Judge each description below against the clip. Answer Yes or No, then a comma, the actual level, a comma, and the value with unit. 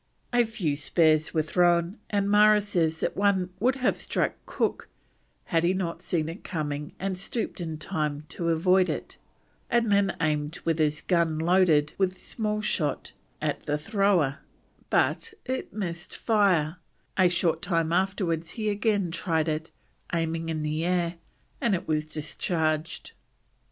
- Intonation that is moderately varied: Yes, average, 3.8 semitones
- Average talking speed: Yes, average, 150 wpm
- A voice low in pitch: No, medium, 170 Hz